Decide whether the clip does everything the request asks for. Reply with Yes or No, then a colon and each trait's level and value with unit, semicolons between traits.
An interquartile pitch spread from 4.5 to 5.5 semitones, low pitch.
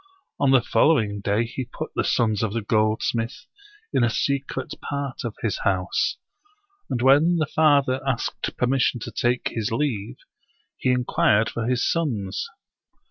No: average, 3.8 semitones; low, 120 Hz